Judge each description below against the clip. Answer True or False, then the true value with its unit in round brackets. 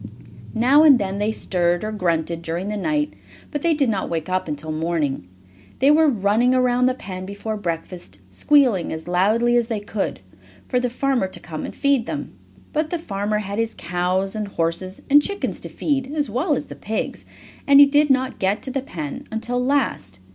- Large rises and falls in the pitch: True (6.5 semitones)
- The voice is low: False (215 Hz)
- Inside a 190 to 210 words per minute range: True (200 wpm)